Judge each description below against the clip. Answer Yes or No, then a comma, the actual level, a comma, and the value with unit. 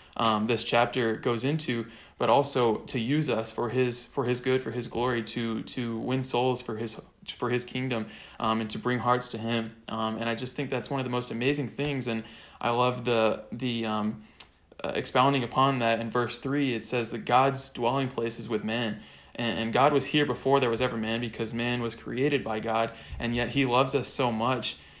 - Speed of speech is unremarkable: No, fast, 220 wpm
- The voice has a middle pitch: No, low, 120 Hz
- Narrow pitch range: Yes, narrow, 2.2 semitones